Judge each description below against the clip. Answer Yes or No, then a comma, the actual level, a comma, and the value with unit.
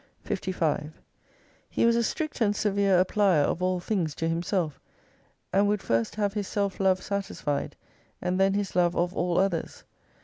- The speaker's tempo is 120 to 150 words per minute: No, average, 165 wpm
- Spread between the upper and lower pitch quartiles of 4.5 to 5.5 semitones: No, average, 2.7 semitones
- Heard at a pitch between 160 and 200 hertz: Yes, medium, 185 Hz